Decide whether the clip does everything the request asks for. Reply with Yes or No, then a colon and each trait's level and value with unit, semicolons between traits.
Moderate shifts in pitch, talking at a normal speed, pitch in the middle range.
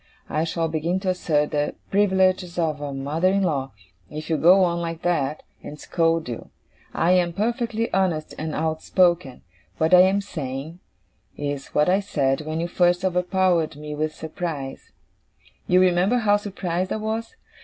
Yes: average, 3.4 semitones; average, 165 wpm; medium, 170 Hz